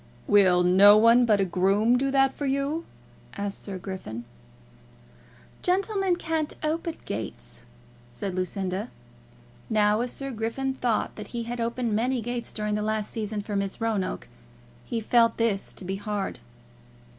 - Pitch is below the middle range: No, high, 220 Hz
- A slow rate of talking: No, average, 150 wpm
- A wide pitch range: No, average, 3.8 semitones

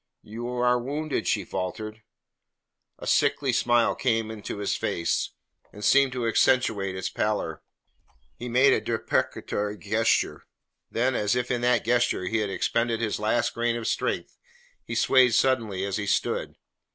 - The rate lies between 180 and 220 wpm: No, average, 150 wpm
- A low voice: Yes, low, 115 Hz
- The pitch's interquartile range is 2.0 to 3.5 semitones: Yes, average, 3.0 semitones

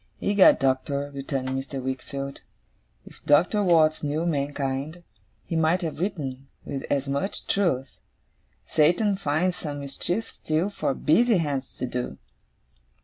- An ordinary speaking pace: No, slow, 130 wpm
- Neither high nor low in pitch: Yes, medium, 145 Hz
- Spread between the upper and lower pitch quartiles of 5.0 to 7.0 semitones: No, average, 4.2 semitones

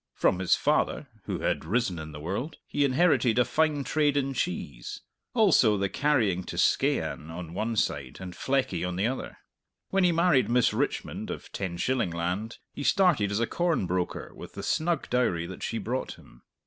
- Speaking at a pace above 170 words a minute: Yes, average, 185 wpm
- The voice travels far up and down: Yes, wide, 8.1 semitones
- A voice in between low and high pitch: No, low, 115 Hz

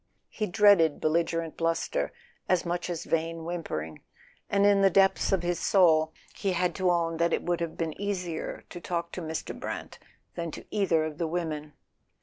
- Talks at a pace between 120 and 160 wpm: No, average, 185 wpm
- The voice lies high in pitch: No, medium, 170 Hz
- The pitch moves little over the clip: Yes, narrow, 2.0 semitones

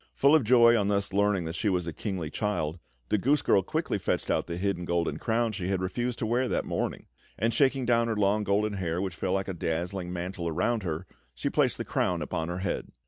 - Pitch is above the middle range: No, very low, 95 Hz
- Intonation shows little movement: No, average, 4.2 semitones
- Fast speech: Yes, fast, 235 wpm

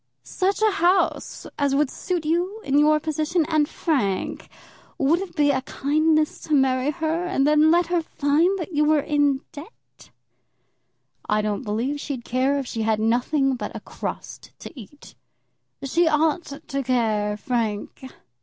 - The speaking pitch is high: Yes, very high, 295 Hz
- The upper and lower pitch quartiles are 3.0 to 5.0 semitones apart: Yes, average, 3.7 semitones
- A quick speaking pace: No, average, 160 wpm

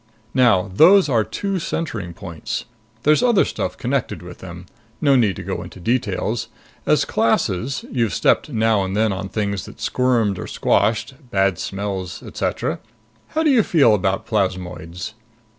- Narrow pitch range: No, average, 5.3 semitones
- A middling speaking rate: Yes, average, 155 wpm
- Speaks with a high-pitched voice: No, low, 105 Hz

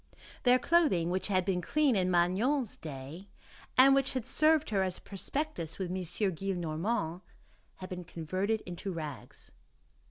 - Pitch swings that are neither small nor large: No, wide, 6.0 semitones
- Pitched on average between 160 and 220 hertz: Yes, high, 190 Hz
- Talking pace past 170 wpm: No, average, 150 wpm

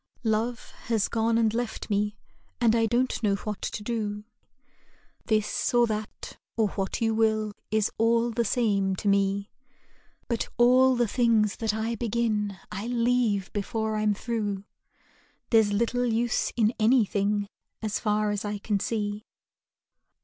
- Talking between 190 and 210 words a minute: No, average, 145 wpm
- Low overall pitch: No, high, 220 Hz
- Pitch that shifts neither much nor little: No, narrow, 2.1 semitones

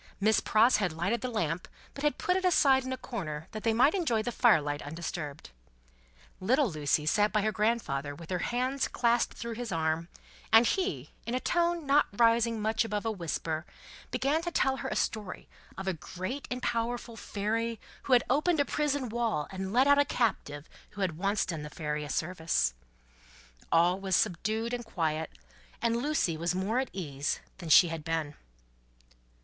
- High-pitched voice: Yes, high, 215 Hz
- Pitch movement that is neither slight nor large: No, wide, 6.9 semitones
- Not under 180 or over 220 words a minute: Yes, average, 190 wpm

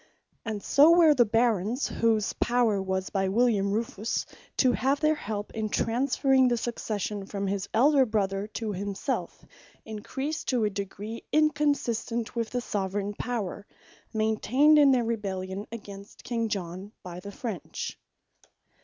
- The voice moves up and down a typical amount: Yes, average, 3.6 semitones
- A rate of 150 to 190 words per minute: No, average, 140 wpm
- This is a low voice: No, high, 220 Hz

